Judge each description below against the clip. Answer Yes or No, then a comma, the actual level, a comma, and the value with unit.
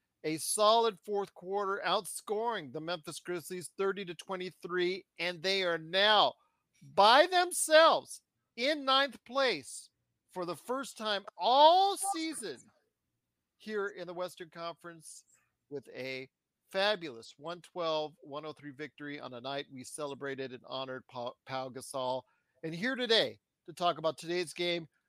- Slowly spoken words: Yes, slow, 125 wpm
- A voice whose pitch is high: No, medium, 175 Hz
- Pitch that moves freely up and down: Yes, wide, 5.8 semitones